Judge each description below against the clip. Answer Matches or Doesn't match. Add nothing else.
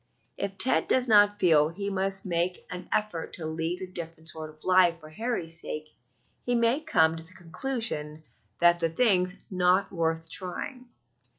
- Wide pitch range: Doesn't match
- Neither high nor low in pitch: Matches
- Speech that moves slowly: Doesn't match